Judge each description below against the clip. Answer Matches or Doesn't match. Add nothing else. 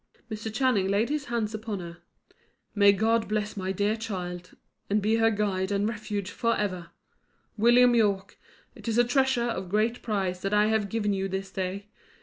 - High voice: Matches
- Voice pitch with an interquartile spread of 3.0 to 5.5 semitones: Doesn't match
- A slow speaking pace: Doesn't match